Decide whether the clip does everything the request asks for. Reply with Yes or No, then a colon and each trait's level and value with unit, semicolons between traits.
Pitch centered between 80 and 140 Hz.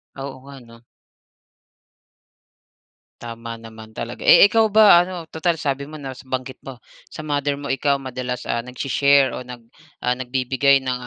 Yes: low, 135 Hz